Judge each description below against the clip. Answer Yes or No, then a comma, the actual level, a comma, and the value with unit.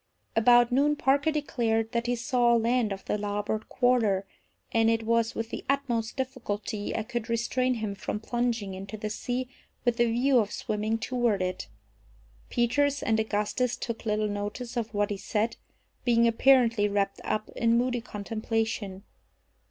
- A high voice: Yes, high, 230 Hz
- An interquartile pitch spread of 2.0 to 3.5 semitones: Yes, narrow, 2.5 semitones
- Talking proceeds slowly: No, average, 160 wpm